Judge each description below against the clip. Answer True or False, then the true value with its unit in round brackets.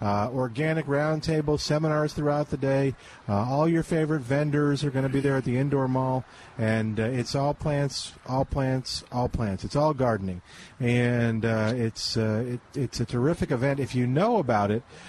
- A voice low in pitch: True (130 Hz)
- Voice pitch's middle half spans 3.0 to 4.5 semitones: True (4.1 semitones)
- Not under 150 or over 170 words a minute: False (185 wpm)